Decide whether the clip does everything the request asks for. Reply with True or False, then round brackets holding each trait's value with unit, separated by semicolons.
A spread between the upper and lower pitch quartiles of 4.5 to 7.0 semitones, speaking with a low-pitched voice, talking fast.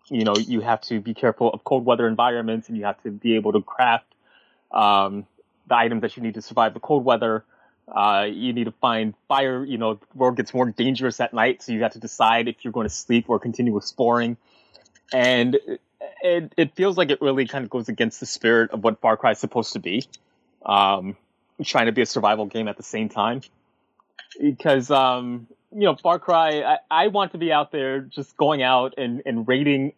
False (3.4 semitones; 120 Hz; 220 wpm)